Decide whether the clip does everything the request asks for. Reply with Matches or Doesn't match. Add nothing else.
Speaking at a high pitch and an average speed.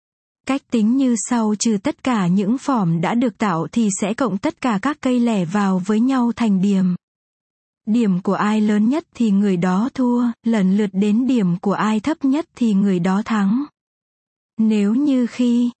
Matches